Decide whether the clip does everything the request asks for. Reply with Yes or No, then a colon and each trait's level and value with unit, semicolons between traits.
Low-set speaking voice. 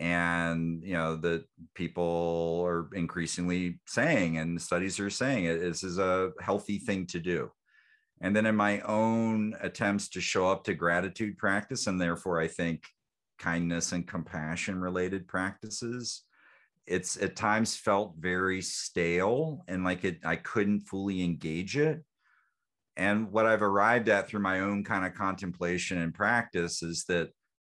Yes: very low, 95 Hz